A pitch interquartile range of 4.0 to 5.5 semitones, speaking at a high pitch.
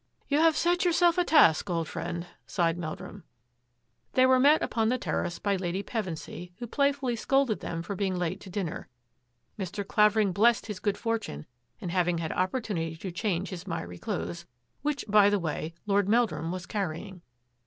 Yes: average, 5.1 semitones; high, 195 Hz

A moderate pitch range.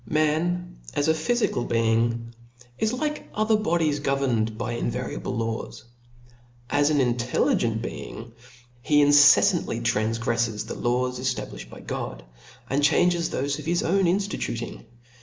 No: wide, 5.8 semitones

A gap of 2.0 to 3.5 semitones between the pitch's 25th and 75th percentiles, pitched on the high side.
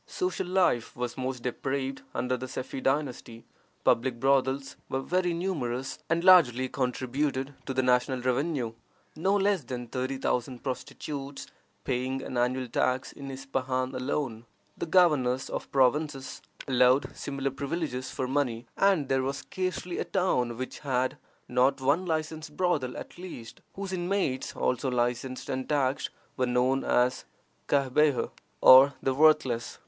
No: average, 2.9 semitones; low, 135 Hz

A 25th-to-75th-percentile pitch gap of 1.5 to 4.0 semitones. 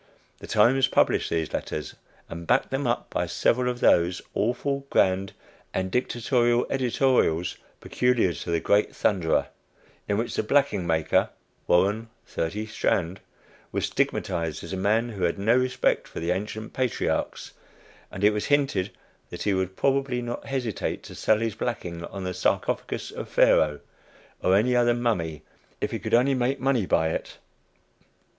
No: average, 5.2 semitones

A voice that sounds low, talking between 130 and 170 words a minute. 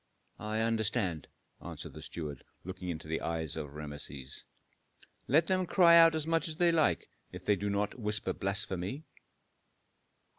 Yes: low, 100 Hz; average, 150 wpm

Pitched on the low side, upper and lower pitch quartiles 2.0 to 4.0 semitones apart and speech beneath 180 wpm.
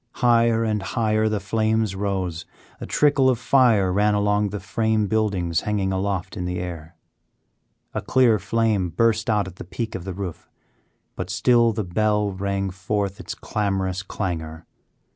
Yes: low, 105 Hz; average, 2.8 semitones; average, 160 wpm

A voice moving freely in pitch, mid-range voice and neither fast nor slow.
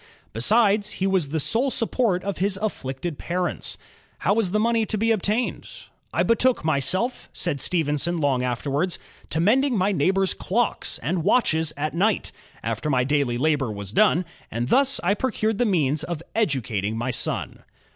Yes: wide, 7.0 semitones; medium, 175 Hz; average, 165 wpm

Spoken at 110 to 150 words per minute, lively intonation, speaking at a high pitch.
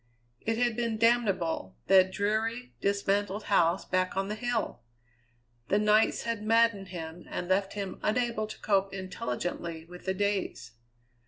No: average, 145 wpm; average, 3.0 semitones; high, 200 Hz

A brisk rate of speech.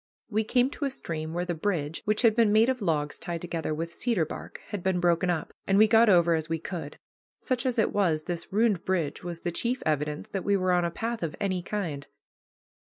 Yes: fast, 235 wpm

